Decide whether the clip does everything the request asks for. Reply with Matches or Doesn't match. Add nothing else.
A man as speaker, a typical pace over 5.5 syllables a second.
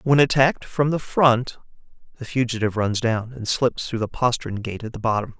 Doesn't match